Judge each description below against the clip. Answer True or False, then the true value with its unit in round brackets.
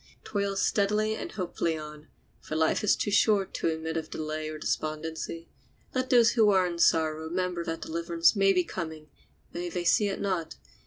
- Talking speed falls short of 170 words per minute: False (180 wpm)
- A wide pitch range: False (3.8 semitones)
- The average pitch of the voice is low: False (170 Hz)